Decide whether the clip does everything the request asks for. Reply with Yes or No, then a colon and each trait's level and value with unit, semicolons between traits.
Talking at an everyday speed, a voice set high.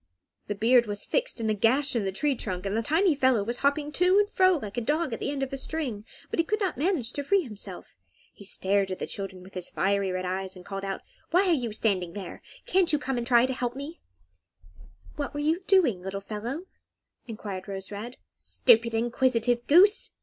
No: fast, 220 wpm; high, 240 Hz